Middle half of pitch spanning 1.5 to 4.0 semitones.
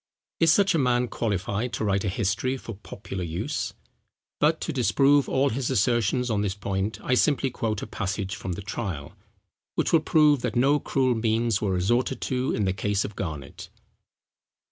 No: average, 5.0 semitones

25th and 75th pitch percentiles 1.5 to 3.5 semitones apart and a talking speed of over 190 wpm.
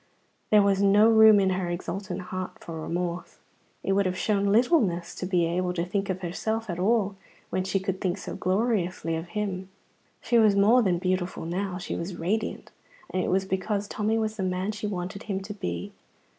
Yes: narrow, 2.5 semitones; average, 200 wpm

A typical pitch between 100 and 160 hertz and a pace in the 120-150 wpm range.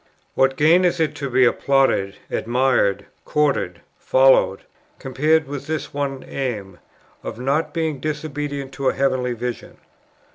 Yes: medium, 140 Hz; slow, 135 wpm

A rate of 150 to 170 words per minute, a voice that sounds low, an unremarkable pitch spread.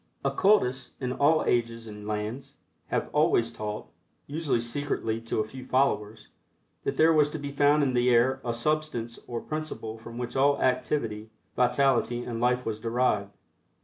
Yes: average, 160 wpm; low, 125 Hz; average, 3.6 semitones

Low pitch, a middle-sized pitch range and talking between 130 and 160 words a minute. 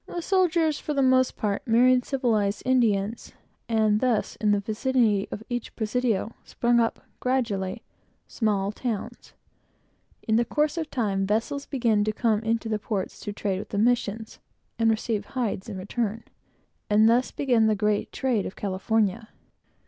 No: high, 225 Hz; average, 3.2 semitones; average, 155 wpm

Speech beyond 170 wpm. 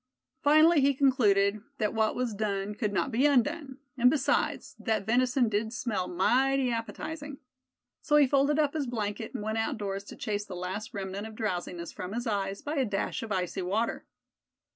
Yes: average, 180 wpm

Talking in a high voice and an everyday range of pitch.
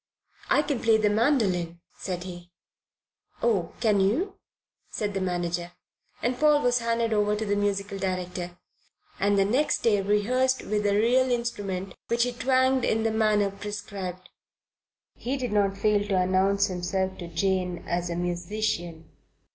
Yes: high, 205 Hz; average, 3.9 semitones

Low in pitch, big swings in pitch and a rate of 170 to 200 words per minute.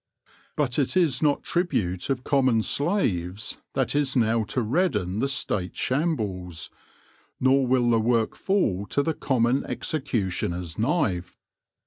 No: low, 125 Hz; wide, 6.0 semitones; slow, 135 wpm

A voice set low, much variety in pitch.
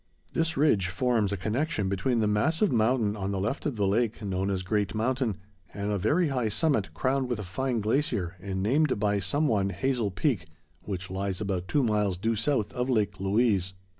No: low, 105 Hz; average, 4.7 semitones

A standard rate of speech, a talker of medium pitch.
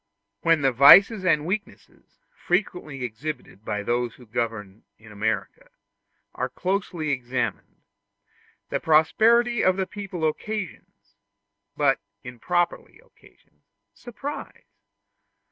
No: slow, 100 wpm; medium, 155 Hz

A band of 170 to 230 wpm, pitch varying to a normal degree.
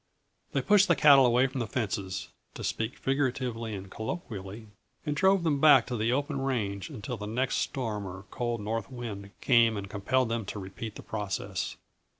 Yes: average, 180 wpm; average, 4.3 semitones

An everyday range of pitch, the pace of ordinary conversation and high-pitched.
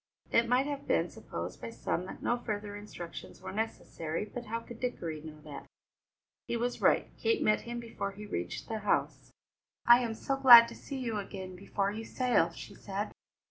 Yes: average, 4.7 semitones; average, 190 wpm; high, 215 Hz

